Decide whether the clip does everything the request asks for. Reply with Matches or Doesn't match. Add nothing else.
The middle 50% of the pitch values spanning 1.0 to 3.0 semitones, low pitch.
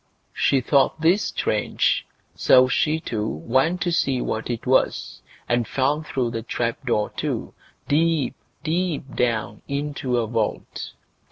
Doesn't match